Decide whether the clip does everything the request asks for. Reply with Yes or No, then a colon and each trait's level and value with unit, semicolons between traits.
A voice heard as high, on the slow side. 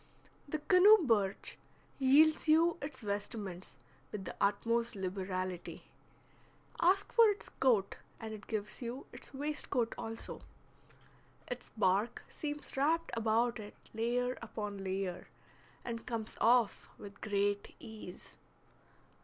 Yes: high, 230 Hz; slow, 115 wpm